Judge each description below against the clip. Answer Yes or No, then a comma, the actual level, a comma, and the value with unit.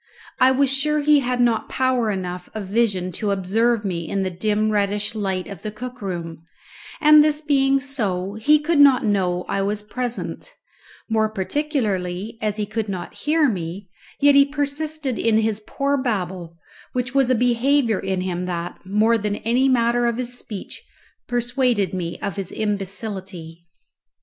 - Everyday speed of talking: Yes, average, 170 wpm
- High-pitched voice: Yes, high, 220 Hz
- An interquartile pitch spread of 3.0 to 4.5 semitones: No, average, 5.0 semitones